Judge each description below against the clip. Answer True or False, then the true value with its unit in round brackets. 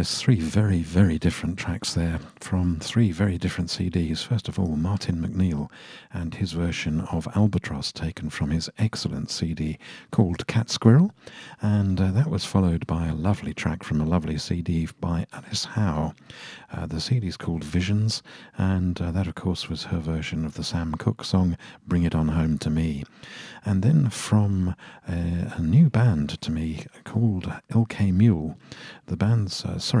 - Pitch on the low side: True (90 Hz)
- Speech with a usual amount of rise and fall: True (4.4 semitones)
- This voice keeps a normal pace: True (175 wpm)